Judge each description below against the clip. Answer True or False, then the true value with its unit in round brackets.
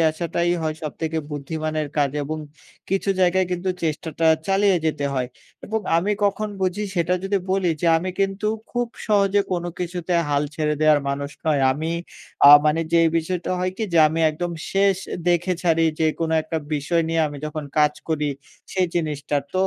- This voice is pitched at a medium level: True (165 Hz)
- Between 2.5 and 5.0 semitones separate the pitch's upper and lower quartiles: True (3.4 semitones)